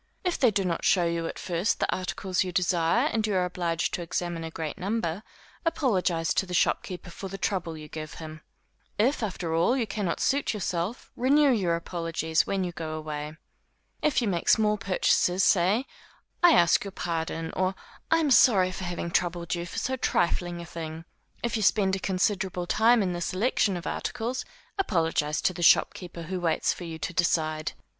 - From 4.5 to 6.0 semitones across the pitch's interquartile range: No, average, 3.7 semitones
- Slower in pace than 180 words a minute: No, average, 190 wpm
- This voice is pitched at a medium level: Yes, medium, 180 Hz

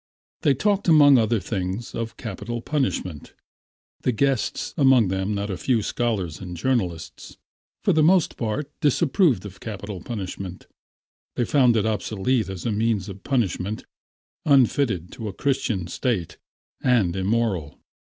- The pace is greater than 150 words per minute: No, average, 140 wpm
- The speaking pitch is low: Yes, low, 110 Hz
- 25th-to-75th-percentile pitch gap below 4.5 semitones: No, wide, 5.5 semitones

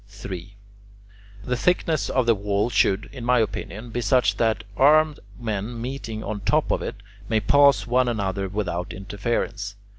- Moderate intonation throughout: Yes, average, 3.8 semitones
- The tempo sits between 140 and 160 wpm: Yes, average, 155 wpm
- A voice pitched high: No, low, 110 Hz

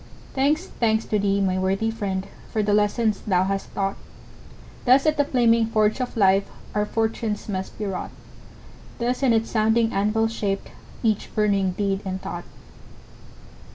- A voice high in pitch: Yes, high, 210 Hz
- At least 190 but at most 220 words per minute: No, average, 155 wpm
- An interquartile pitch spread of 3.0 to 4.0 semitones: No, narrow, 2.6 semitones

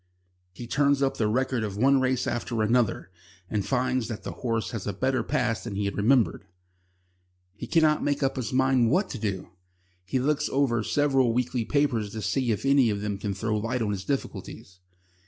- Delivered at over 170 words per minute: Yes, average, 195 wpm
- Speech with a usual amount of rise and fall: Yes, average, 3.9 semitones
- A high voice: No, low, 120 Hz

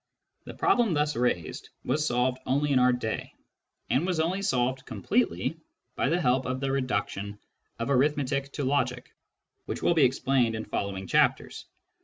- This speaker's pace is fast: No, average, 165 wpm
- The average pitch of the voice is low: Yes, low, 130 Hz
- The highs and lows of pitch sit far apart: No, average, 3.1 semitones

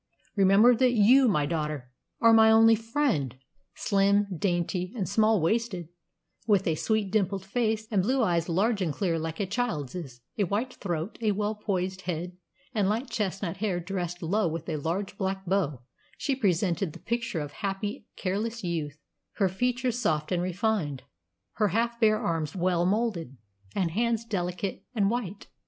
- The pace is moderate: Yes, average, 165 wpm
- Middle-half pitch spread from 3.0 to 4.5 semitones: Yes, average, 4.2 semitones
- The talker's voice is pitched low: No, high, 195 Hz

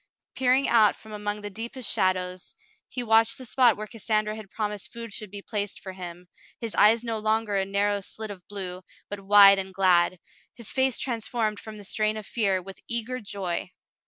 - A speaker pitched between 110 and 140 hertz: No, high, 210 Hz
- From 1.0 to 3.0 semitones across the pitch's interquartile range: Yes, narrow, 2.5 semitones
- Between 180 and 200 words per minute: Yes, average, 190 wpm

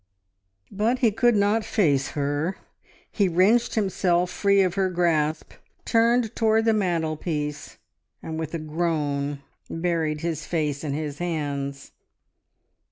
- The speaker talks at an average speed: No, slow, 125 wpm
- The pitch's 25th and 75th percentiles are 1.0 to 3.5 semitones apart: No, average, 4.9 semitones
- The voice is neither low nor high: Yes, medium, 170 Hz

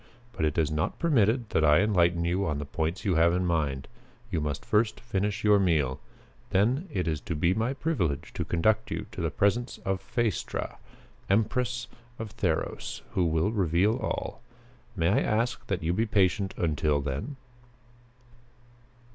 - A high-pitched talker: No, very low, 95 Hz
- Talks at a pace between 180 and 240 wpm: No, average, 165 wpm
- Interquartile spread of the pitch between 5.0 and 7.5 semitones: Yes, wide, 5.4 semitones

